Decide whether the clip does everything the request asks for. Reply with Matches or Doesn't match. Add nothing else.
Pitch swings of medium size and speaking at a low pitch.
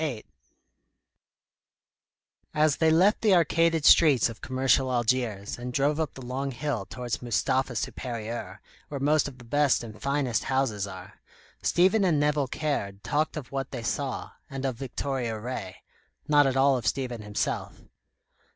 Matches